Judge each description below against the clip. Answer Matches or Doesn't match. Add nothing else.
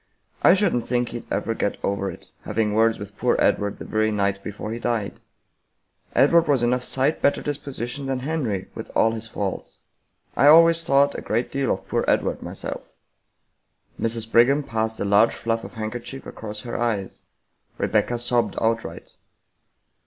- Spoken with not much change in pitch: Doesn't match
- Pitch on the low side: Matches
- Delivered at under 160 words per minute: Doesn't match